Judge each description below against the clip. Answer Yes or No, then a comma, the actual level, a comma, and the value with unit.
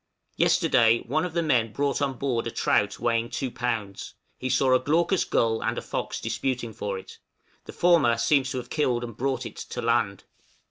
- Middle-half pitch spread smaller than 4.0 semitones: Yes, average, 3.2 semitones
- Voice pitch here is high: No, low, 125 Hz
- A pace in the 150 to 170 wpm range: No, average, 195 wpm